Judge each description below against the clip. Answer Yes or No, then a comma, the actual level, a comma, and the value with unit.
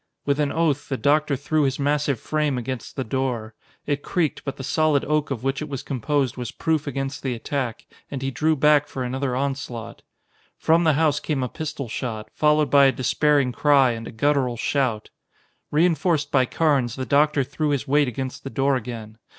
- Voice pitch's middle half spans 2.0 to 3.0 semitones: Yes, narrow, 2.6 semitones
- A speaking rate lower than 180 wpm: No, average, 195 wpm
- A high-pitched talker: No, medium, 140 Hz